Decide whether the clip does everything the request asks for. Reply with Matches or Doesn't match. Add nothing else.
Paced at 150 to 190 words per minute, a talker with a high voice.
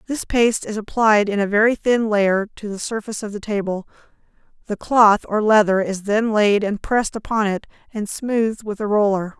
Doesn't match